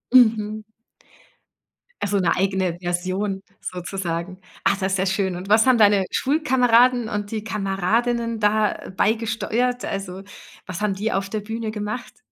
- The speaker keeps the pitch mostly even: No, average, 3.0 semitones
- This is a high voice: Yes, high, 210 Hz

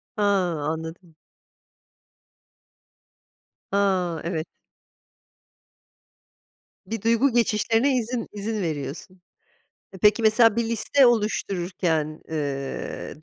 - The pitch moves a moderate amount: No, wide, 5.8 semitones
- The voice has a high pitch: Yes, high, 200 Hz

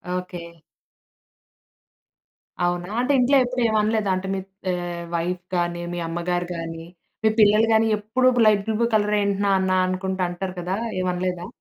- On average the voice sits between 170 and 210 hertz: Yes, medium, 185 Hz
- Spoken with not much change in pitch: No, average, 3.2 semitones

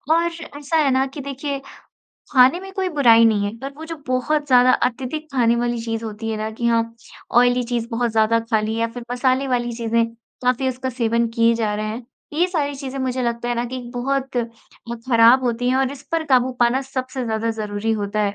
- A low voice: No, high, 245 Hz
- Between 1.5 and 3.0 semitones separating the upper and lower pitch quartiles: Yes, narrow, 2.6 semitones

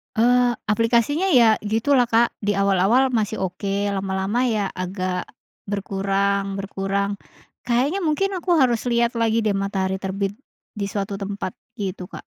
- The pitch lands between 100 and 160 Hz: No, high, 205 Hz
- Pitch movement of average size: Yes, average, 3.3 semitones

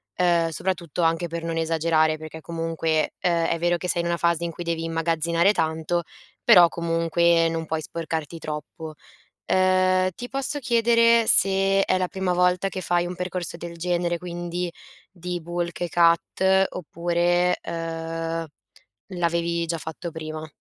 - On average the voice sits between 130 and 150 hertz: No, medium, 170 Hz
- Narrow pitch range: Yes, narrow, 1.6 semitones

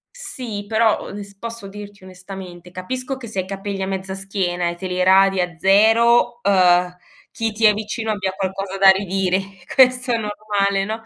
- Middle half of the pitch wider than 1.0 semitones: Yes, narrow, 2.6 semitones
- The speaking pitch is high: Yes, high, 195 Hz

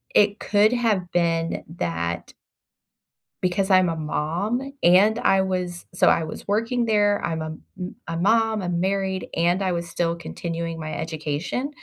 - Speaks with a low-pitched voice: No, medium, 180 Hz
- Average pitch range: Yes, average, 3.6 semitones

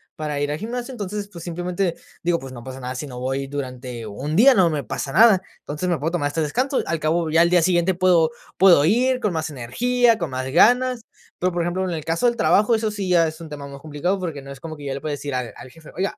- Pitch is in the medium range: Yes, medium, 165 Hz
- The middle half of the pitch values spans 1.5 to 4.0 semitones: No, average, 4.8 semitones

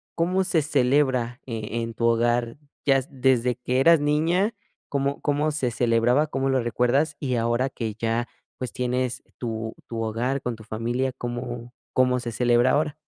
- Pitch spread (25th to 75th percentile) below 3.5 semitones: Yes, average, 2.9 semitones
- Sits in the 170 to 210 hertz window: No, low, 125 Hz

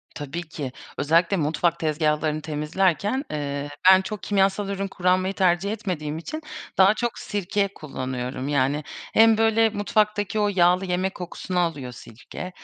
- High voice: No, medium, 180 Hz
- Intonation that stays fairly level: No, average, 4.9 semitones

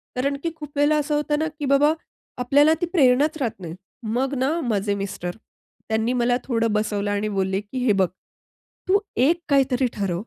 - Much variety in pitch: Yes, wide, 5.9 semitones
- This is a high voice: Yes, very high, 255 Hz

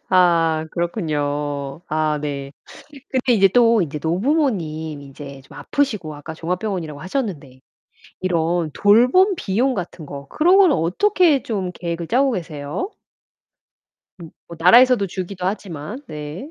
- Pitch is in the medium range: Yes, medium, 175 Hz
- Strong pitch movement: Yes, wide, 7.2 semitones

